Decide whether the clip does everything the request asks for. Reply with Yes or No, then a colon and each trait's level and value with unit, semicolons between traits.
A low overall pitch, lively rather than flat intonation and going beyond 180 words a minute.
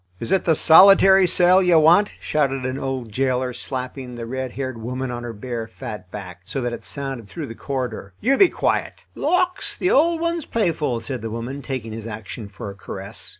Yes: low, 130 Hz; wide, 6.1 semitones; average, 200 wpm